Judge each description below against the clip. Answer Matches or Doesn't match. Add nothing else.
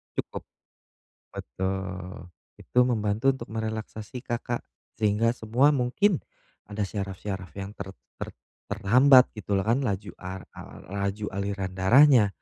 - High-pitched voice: Doesn't match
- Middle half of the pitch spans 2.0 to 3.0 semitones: Doesn't match